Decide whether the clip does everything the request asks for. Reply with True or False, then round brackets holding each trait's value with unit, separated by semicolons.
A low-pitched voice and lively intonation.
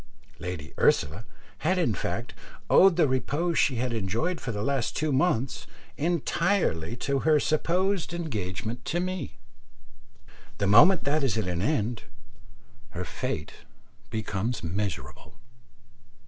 True (130 Hz; 8.0 semitones)